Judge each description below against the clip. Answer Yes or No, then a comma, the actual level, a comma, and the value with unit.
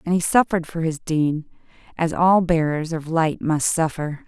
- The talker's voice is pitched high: No, medium, 165 Hz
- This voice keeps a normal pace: Yes, average, 185 wpm